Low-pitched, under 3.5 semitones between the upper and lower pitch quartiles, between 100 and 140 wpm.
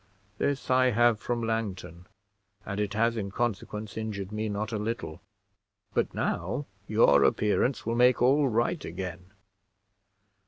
Yes: low, 110 Hz; average, 3.1 semitones; slow, 135 wpm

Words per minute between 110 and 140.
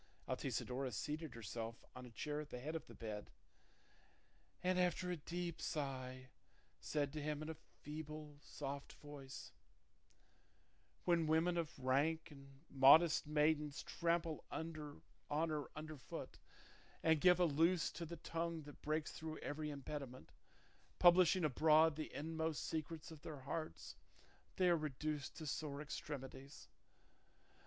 Yes: slow, 135 wpm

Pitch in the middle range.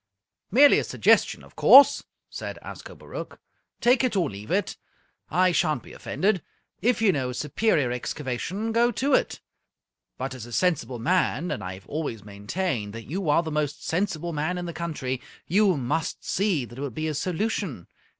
Yes: medium, 160 Hz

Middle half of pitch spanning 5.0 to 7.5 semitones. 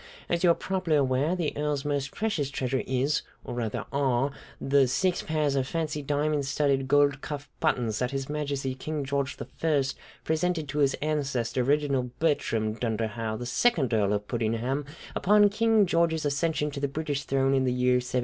No: average, 3.1 semitones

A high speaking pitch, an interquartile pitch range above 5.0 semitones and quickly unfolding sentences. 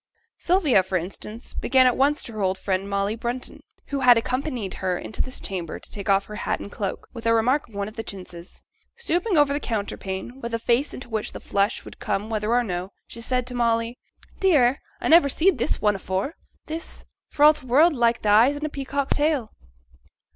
Yes: high, 235 Hz; wide, 5.5 semitones; fast, 215 wpm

